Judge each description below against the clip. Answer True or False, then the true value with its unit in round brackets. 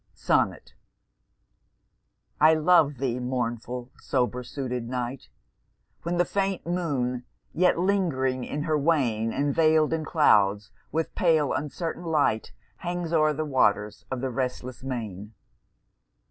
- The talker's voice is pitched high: False (140 Hz)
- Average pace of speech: False (120 wpm)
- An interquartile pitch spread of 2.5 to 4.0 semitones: False (4.7 semitones)